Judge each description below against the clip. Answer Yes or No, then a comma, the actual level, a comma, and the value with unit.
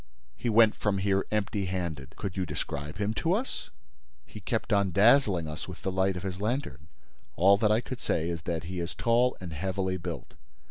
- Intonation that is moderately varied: Yes, average, 3.7 semitones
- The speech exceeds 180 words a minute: Yes, average, 200 wpm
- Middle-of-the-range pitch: No, very low, 95 Hz